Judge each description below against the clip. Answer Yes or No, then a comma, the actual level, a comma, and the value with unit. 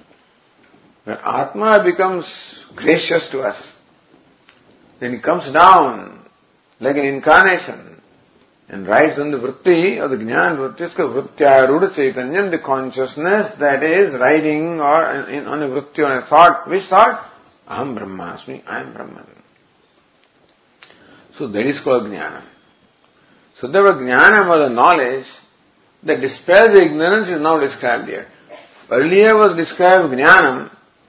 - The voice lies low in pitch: No, medium, 155 Hz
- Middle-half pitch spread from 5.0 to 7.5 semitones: Yes, average, 5.3 semitones